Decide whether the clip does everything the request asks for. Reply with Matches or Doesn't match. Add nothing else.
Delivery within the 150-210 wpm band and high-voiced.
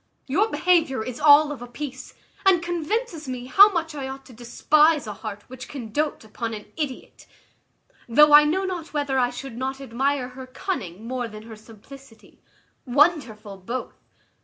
Matches